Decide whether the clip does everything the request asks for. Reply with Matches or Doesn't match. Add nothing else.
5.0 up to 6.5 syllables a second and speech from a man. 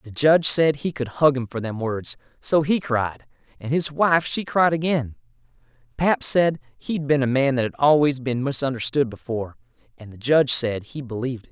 Matches